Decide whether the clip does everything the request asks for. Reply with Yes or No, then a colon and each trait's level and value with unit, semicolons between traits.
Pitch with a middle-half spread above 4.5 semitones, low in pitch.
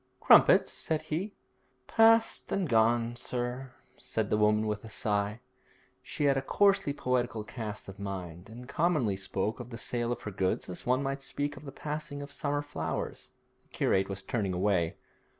Yes: wide, 5.6 semitones; low, 120 Hz